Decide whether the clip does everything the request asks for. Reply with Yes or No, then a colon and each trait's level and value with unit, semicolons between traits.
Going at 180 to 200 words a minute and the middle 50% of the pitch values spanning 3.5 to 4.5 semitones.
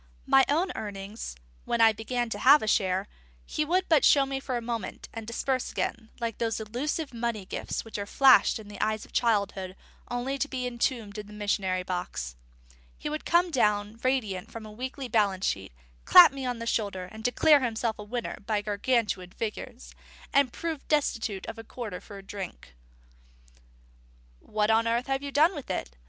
Yes: average, 190 wpm; average, 4.1 semitones